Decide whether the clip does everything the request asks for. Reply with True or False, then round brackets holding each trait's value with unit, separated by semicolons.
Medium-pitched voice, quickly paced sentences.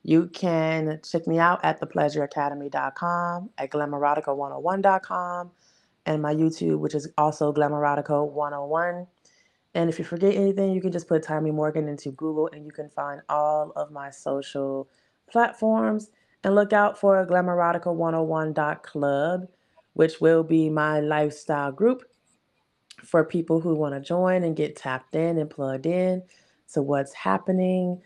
False (160 Hz; 140 wpm)